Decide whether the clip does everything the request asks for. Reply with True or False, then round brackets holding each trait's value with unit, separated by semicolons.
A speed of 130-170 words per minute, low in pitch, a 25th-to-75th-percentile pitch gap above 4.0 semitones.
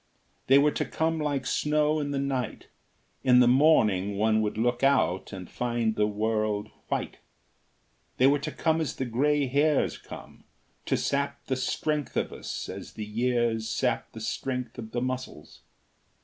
True (165 wpm; 125 Hz; 4.4 semitones)